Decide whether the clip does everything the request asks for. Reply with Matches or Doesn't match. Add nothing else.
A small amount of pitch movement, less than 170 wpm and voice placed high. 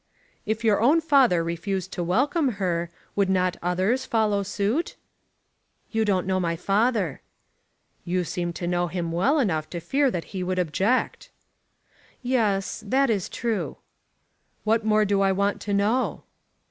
Doesn't match